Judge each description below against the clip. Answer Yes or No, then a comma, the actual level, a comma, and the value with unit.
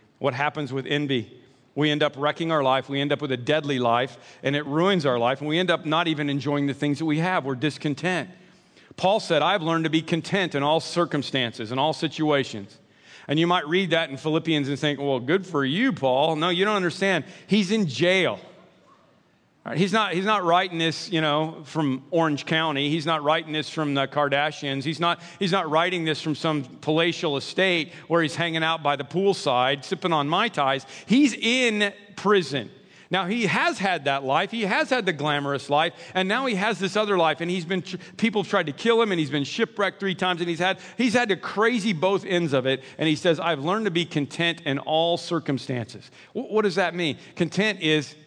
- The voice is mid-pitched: Yes, medium, 160 Hz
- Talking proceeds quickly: Yes, fast, 215 wpm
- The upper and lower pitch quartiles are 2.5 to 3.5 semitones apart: No, average, 4.4 semitones